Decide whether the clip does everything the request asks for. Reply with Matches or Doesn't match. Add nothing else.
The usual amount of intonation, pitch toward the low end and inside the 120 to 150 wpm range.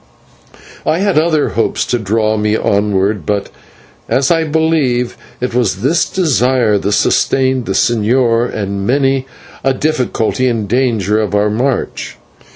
Matches